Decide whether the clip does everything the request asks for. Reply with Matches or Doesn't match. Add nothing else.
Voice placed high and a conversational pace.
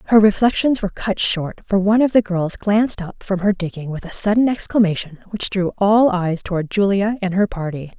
Doesn't match